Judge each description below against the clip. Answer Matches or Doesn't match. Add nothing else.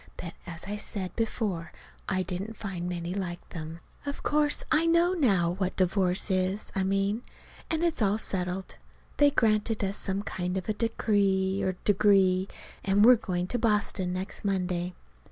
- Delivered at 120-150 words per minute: Doesn't match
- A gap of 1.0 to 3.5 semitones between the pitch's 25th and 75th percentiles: Matches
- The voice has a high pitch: Matches